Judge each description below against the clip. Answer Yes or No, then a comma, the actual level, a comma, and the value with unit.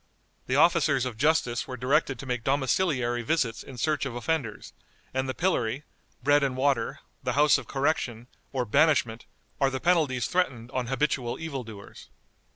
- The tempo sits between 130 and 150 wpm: No, average, 160 wpm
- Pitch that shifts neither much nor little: Yes, average, 3.3 semitones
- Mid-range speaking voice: No, low, 130 Hz